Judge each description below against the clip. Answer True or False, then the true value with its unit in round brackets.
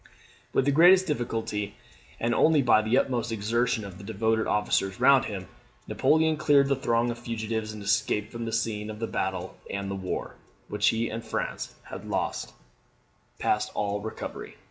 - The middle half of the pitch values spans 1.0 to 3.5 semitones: True (3.0 semitones)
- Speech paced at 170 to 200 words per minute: True (175 wpm)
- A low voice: True (115 Hz)